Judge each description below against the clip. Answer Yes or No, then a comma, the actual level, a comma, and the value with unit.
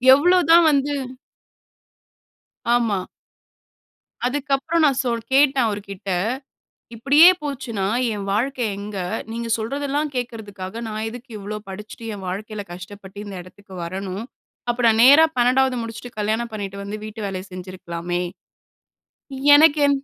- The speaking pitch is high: Yes, high, 225 Hz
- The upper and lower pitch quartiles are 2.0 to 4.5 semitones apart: No, average, 5.3 semitones